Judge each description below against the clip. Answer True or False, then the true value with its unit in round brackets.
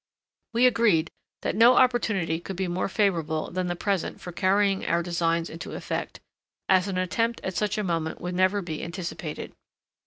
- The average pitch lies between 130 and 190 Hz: True (185 Hz)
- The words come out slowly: False (175 wpm)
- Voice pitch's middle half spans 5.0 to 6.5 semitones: False (3.2 semitones)